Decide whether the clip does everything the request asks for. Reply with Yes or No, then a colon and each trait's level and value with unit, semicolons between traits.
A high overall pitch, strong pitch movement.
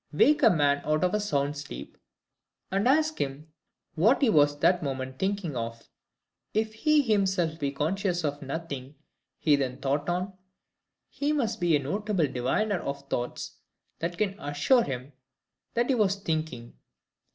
No: medium, 160 Hz; wide, 6.4 semitones